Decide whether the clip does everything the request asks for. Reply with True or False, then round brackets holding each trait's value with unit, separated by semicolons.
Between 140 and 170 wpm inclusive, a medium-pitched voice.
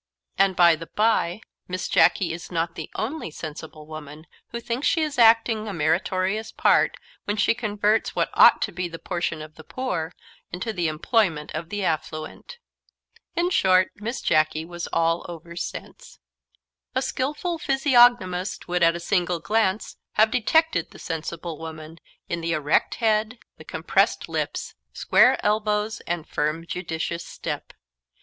True (155 wpm; 180 Hz)